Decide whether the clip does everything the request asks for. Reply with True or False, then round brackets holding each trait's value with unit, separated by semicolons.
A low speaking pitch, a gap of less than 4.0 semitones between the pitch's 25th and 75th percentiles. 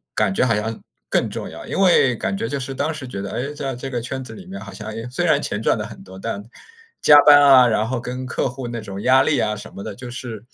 True (125 Hz; 3.6 semitones)